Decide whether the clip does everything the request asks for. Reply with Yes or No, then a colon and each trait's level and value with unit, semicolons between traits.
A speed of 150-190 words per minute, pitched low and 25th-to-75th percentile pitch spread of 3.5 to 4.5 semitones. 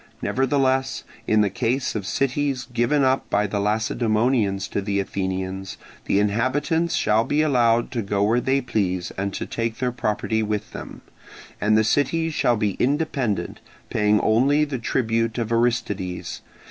Yes: average, 155 wpm; low, 115 Hz; average, 4.2 semitones